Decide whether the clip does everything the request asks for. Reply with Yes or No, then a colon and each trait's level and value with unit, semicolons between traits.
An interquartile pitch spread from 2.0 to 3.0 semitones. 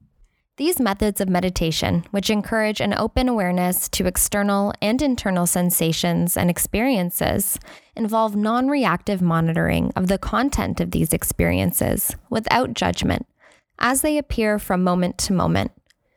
No: average, 4.2 semitones